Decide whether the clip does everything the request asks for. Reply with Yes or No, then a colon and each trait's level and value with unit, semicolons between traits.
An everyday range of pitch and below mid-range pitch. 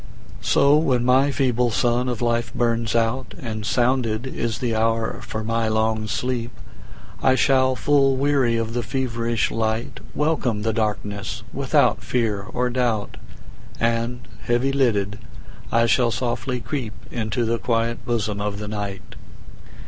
No: narrow, 2.3 semitones; low, 115 Hz